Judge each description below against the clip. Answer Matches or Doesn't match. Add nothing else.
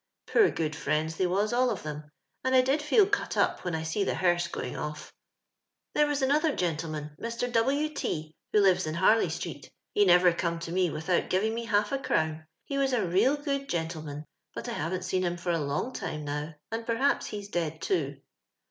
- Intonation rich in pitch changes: Matches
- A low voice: Doesn't match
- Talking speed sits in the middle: Doesn't match